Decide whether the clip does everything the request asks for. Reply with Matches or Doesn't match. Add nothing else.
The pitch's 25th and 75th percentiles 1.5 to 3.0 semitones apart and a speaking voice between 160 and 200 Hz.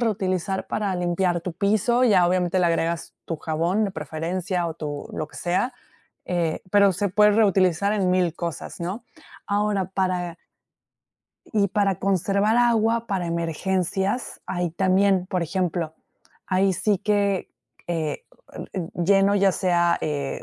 Matches